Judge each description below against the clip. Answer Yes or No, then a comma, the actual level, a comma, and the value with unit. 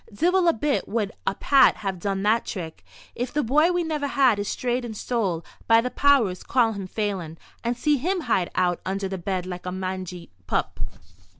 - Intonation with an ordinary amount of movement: No, wide, 6.4 semitones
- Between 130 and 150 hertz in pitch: No, high, 215 Hz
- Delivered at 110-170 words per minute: No, average, 200 wpm